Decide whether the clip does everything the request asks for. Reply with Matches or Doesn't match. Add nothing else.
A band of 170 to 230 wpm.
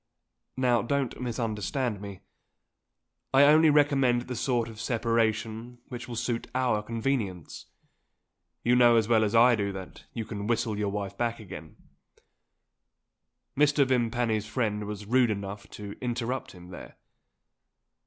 Doesn't match